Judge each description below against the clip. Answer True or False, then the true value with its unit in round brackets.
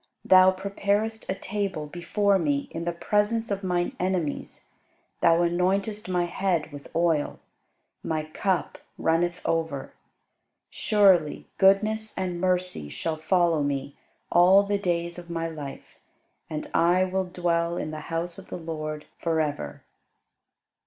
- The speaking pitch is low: False (175 Hz)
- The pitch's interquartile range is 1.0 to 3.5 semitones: True (2.8 semitones)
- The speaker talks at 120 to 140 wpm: True (135 wpm)